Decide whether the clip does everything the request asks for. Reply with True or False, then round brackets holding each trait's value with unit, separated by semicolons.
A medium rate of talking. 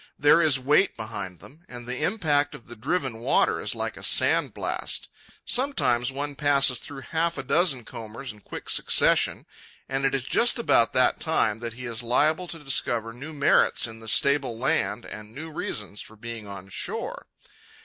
True (180 wpm)